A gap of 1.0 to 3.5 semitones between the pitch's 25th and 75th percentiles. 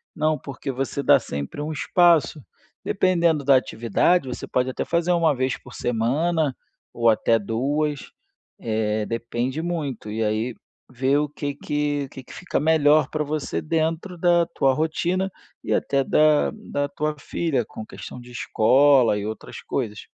No: average, 4.4 semitones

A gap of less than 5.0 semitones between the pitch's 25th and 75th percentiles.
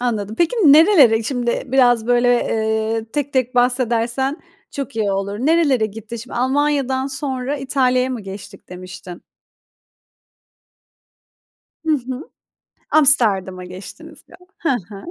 Yes: average, 3.7 semitones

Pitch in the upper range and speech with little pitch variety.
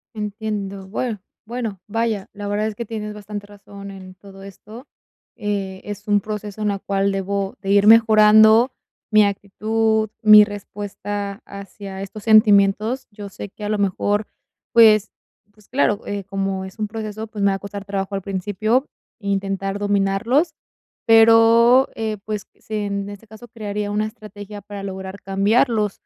Yes: high, 205 Hz; narrow, 1.5 semitones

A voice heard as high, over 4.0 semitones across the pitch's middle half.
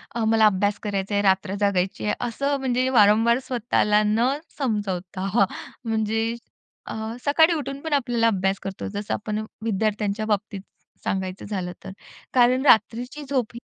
No: high, 215 Hz; average, 3.3 semitones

